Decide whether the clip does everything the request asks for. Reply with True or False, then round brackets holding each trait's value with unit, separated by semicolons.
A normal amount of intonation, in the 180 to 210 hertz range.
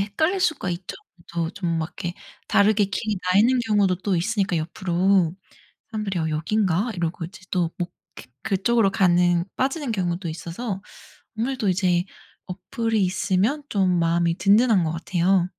True (3.5 semitones; 190 Hz)